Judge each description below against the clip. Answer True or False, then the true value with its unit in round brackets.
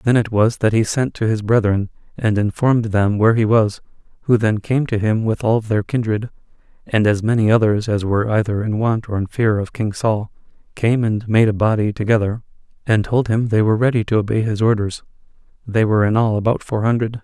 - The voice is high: False (110 Hz)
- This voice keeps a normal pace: False (215 wpm)